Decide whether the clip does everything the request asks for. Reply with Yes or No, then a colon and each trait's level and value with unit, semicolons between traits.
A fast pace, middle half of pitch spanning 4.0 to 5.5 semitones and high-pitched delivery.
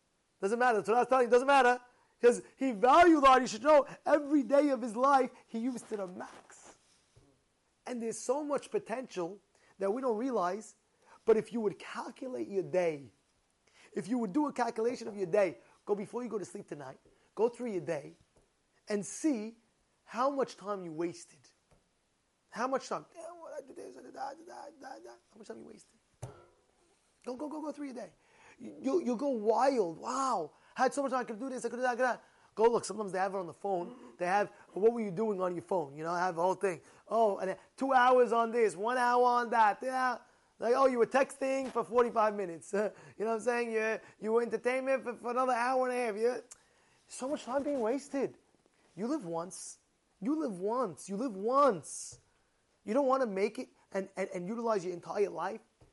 Yes: fast, 210 wpm; average, 4.3 semitones; high, 235 Hz